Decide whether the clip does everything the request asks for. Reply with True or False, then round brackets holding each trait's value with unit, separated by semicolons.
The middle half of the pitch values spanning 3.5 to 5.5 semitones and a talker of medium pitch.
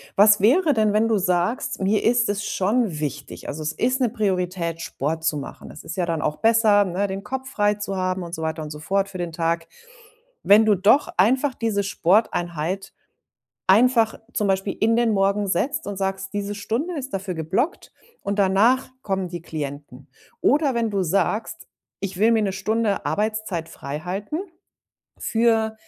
False (4.1 semitones; 200 Hz)